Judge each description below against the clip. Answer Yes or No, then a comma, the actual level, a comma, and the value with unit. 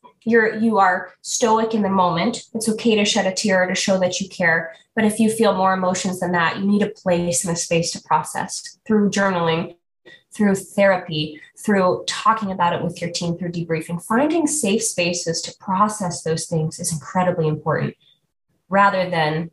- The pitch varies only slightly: No, average, 3.6 semitones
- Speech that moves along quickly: No, average, 185 wpm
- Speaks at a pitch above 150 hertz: Yes, medium, 185 Hz